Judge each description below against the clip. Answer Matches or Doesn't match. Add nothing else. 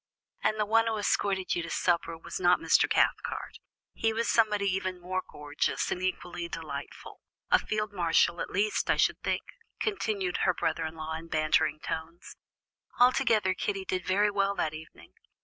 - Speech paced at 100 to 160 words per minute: Doesn't match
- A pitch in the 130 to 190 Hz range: Matches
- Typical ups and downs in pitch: Matches